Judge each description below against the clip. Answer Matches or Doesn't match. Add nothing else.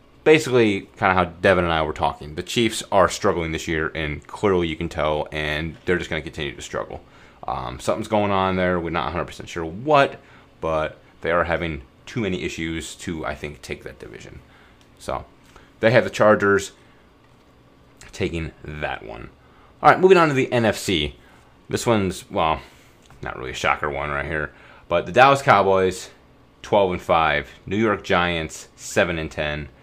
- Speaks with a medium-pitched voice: Doesn't match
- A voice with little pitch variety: Doesn't match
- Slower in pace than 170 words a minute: Doesn't match